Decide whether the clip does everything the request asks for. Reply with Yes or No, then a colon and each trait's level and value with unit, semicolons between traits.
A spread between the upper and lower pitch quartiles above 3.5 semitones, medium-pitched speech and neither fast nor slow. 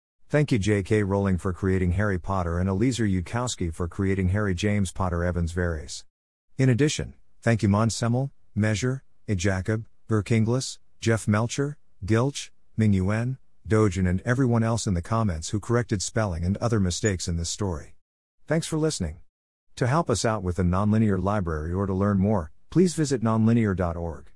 No: average, 4.1 semitones; low, 105 Hz; average, 165 wpm